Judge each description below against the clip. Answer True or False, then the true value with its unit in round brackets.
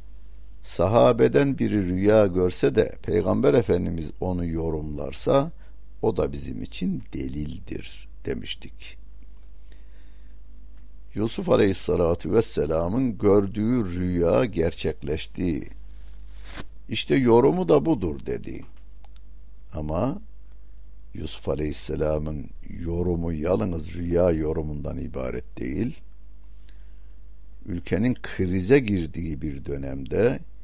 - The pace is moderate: False (80 wpm)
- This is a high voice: False (85 Hz)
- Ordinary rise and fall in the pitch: True (4.4 semitones)